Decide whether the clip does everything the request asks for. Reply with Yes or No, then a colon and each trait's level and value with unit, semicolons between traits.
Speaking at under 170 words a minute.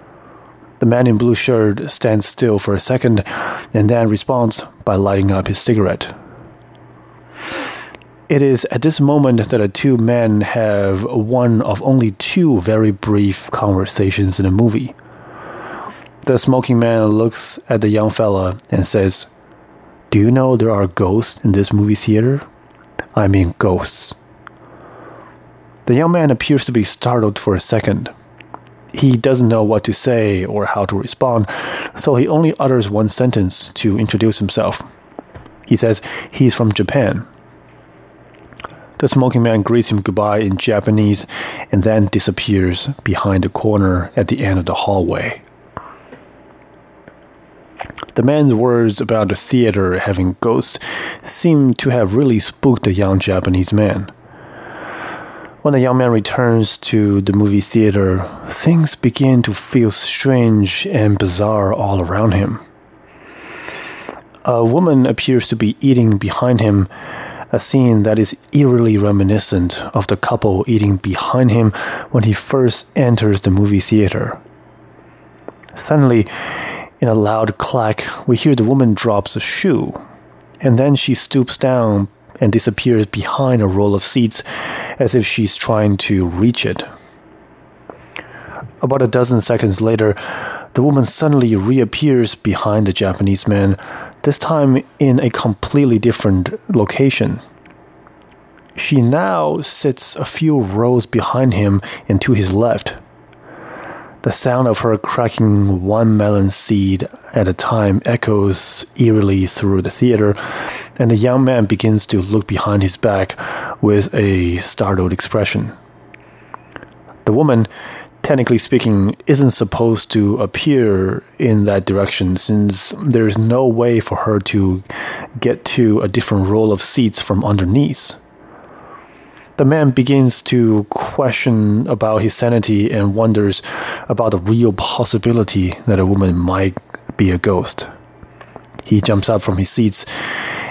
Yes: average, 140 wpm